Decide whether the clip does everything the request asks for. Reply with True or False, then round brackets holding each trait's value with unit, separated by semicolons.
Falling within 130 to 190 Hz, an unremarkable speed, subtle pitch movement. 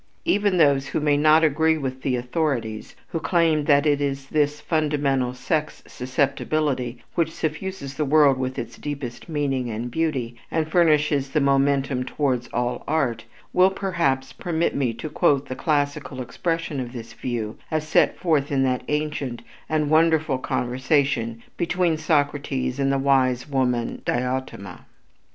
False (140 Hz; 150 wpm; 3.4 semitones)